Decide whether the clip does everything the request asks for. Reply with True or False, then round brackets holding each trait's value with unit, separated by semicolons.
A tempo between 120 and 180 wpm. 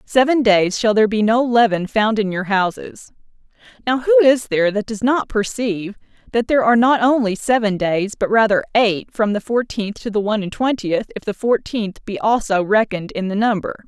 False (200 wpm)